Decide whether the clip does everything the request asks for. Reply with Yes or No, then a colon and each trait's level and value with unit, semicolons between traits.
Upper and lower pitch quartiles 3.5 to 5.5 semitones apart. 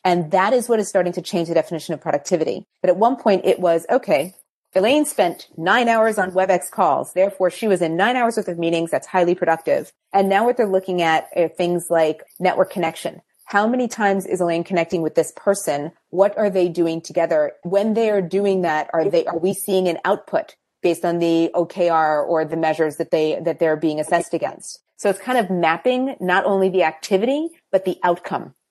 No: average, 3.1 semitones